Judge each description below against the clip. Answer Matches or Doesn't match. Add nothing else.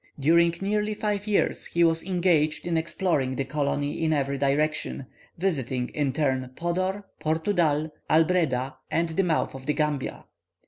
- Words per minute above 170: Doesn't match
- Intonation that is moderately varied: Matches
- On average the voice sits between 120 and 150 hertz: Doesn't match